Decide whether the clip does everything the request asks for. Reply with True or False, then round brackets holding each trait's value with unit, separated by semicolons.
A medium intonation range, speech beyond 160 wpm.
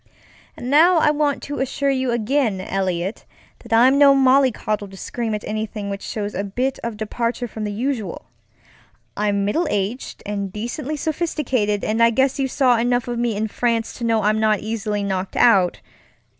True (4.1 semitones; 180 wpm)